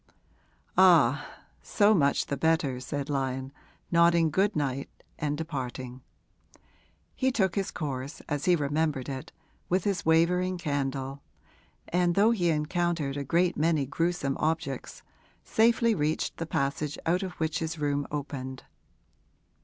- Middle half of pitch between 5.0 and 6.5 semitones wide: No, average, 3.9 semitones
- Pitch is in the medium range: Yes, medium, 155 Hz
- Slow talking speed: Yes, slow, 130 wpm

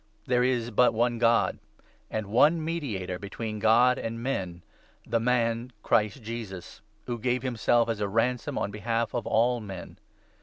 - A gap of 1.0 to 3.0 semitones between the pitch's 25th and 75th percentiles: Yes, narrow, 2.4 semitones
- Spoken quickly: No, average, 165 wpm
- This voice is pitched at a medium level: No, low, 115 Hz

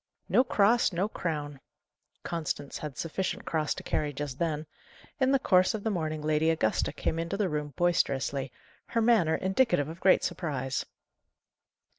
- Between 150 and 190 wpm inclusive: Yes, average, 155 wpm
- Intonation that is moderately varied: Yes, average, 4.4 semitones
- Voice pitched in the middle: Yes, medium, 165 Hz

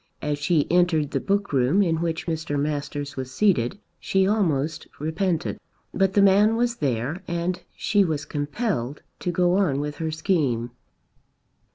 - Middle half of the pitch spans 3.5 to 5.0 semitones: Yes, average, 4.7 semitones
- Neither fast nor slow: Yes, average, 155 wpm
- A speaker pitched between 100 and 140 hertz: No, medium, 160 Hz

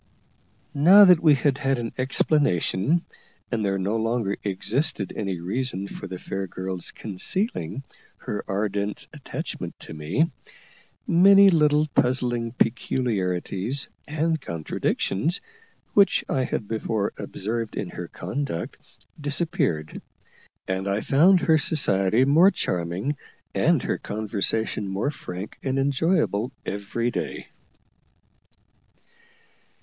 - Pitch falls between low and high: No, low, 115 Hz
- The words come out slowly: Yes, slow, 110 wpm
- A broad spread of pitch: Yes, wide, 7.0 semitones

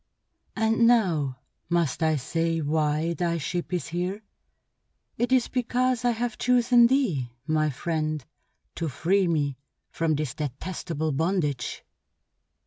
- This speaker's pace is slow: Yes, slow, 125 wpm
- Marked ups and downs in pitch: Yes, wide, 6.4 semitones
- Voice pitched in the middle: Yes, medium, 170 Hz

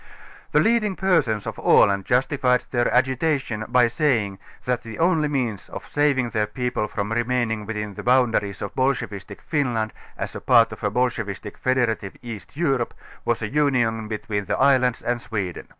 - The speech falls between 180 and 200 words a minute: No, average, 170 wpm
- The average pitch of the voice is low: Yes, low, 120 Hz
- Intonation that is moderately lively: Yes, average, 3.5 semitones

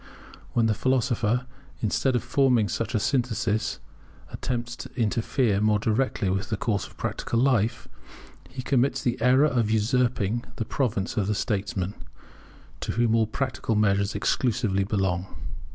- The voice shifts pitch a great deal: No, average, 3.2 semitones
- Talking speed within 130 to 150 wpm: Yes, average, 145 wpm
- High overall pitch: No, low, 115 Hz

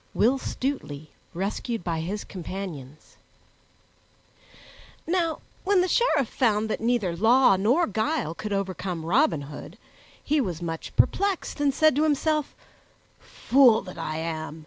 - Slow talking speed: Yes, slow, 130 wpm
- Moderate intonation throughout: No, wide, 8.9 semitones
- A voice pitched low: No, high, 215 Hz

